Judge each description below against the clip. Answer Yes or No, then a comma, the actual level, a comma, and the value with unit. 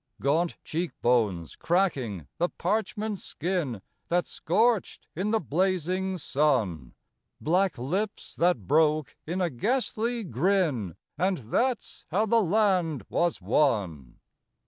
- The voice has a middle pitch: Yes, medium, 175 Hz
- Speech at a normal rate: No, slow, 115 wpm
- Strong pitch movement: Yes, wide, 6.7 semitones